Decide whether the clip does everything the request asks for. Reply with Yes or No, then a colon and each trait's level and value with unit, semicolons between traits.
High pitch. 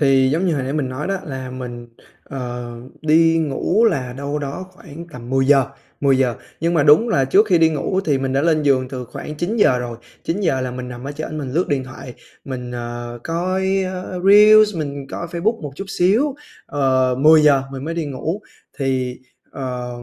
No: medium, 145 Hz